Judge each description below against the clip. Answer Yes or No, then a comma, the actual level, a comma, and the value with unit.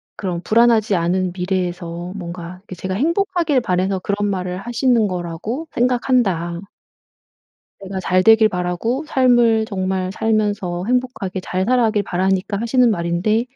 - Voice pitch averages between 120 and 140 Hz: No, high, 195 Hz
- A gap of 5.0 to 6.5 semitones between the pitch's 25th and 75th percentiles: No, average, 4.4 semitones